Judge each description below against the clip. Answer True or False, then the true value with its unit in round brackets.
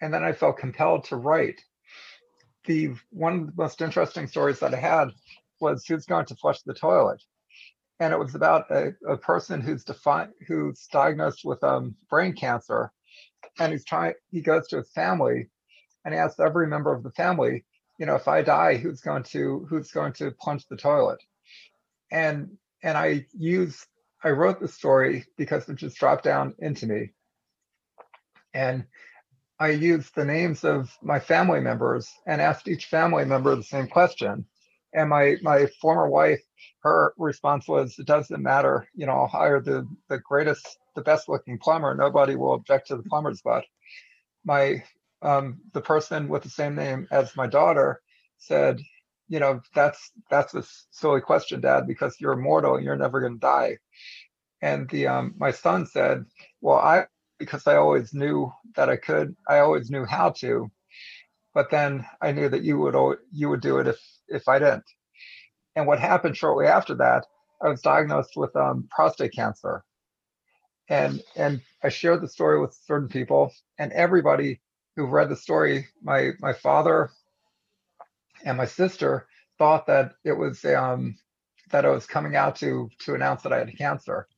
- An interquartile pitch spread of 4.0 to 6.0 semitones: True (4.6 semitones)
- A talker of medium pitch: True (145 Hz)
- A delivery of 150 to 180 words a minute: True (175 wpm)